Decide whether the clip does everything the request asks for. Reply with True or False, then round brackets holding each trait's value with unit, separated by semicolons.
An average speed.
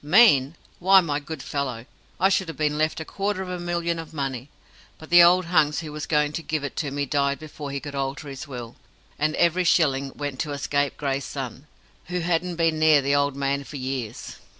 False (220 wpm)